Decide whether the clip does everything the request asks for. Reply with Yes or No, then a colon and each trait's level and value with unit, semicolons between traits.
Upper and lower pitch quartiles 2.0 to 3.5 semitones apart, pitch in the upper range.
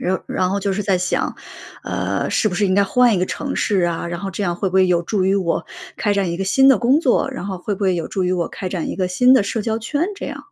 Yes: average, 2.9 semitones; high, 195 Hz